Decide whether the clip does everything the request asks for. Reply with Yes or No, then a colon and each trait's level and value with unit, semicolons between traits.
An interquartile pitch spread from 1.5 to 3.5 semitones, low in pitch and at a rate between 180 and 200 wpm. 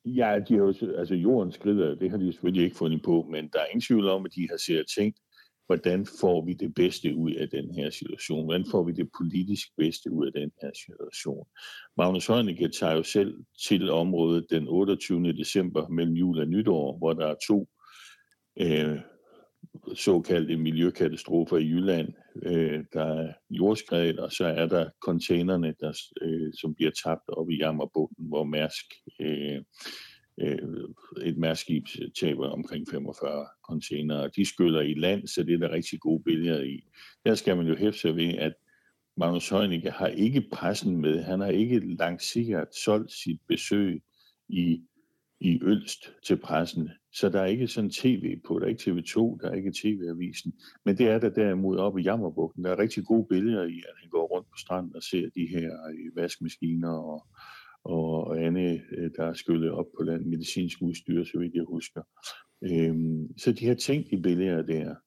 Yes: average, 3.1 semitones; very low, 85 Hz; average, 185 wpm